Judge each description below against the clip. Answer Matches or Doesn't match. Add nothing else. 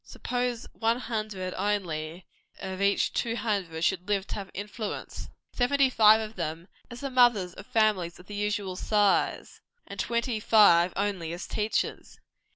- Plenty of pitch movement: Doesn't match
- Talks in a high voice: Matches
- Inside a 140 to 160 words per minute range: Matches